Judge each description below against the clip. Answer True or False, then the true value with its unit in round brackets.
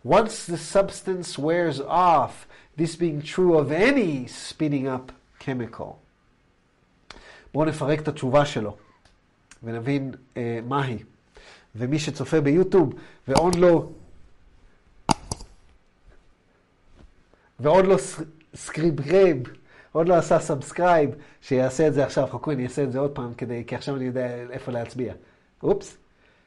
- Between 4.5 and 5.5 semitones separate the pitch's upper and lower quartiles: True (5.0 semitones)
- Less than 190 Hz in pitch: True (140 Hz)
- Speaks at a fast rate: False (115 wpm)